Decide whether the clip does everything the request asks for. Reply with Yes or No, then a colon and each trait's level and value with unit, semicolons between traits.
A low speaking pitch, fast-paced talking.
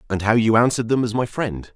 Yes: low, 115 Hz; fast, 275 wpm